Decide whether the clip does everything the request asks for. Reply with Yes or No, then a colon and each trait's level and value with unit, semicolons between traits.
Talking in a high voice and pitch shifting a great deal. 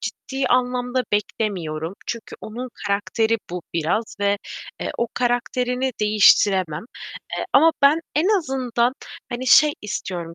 No: high, 235 Hz; average, 4.0 semitones